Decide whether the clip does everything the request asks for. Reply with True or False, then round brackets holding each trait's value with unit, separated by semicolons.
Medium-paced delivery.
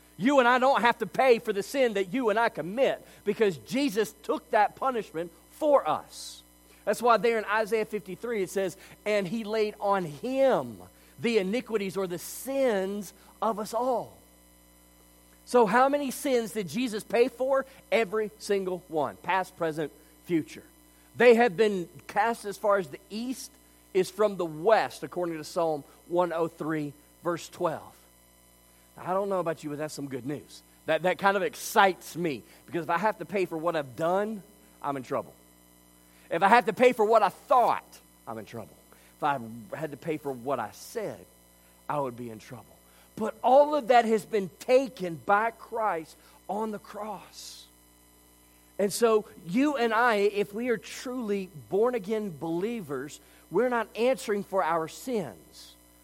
True (170 wpm)